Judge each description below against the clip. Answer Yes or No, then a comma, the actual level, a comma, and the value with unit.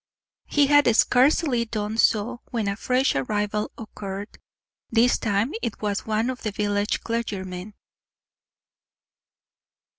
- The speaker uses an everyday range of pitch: Yes, average, 3.0 semitones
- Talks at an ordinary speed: No, slow, 115 wpm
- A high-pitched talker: Yes, high, 215 Hz